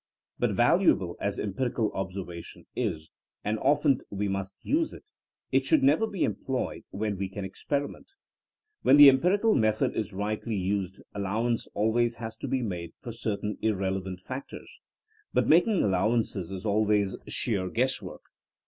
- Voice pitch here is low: Yes, low, 110 Hz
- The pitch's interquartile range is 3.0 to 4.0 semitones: No, average, 4.9 semitones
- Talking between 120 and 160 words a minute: Yes, average, 155 wpm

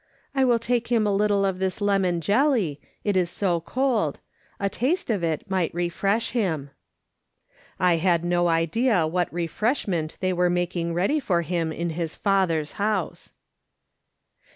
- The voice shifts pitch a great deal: No, average, 3.8 semitones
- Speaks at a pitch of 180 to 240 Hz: Yes, medium, 185 Hz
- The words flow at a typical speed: Yes, average, 155 wpm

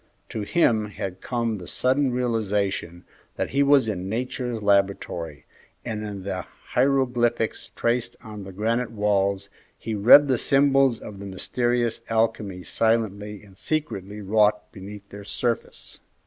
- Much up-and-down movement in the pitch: No, average, 3.4 semitones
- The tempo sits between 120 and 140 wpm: Yes, slow, 135 wpm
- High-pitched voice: No, low, 110 Hz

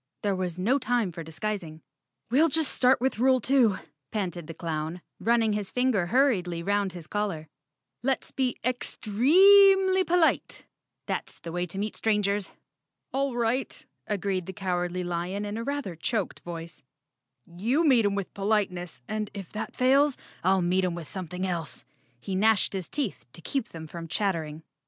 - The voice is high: Yes, high, 200 Hz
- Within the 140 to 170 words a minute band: Yes, average, 165 wpm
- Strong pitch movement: Yes, wide, 6.0 semitones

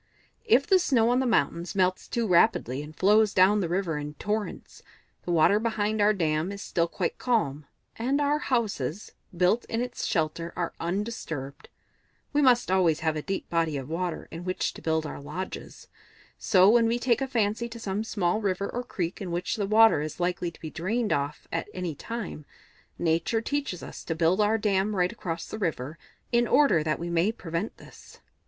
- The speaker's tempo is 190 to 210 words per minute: Yes, average, 195 wpm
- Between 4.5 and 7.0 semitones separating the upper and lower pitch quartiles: Yes, average, 5.2 semitones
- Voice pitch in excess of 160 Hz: Yes, high, 190 Hz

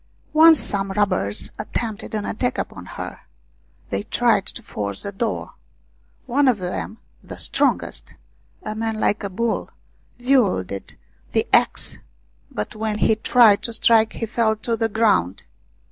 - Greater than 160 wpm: No, average, 145 wpm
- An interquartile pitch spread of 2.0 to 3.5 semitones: Yes, narrow, 2.6 semitones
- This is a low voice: No, high, 220 Hz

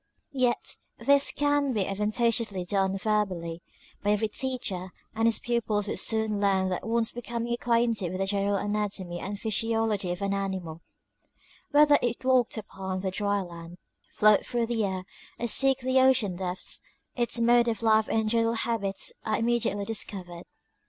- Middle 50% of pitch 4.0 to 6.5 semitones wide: No, average, 3.5 semitones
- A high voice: Yes, high, 215 Hz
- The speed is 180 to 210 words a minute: No, average, 160 wpm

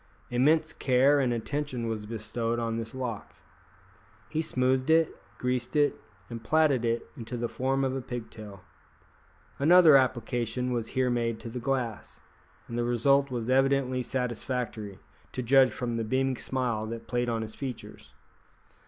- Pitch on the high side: No, low, 125 Hz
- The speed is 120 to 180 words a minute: Yes, average, 155 wpm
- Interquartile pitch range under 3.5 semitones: Yes, narrow, 2.4 semitones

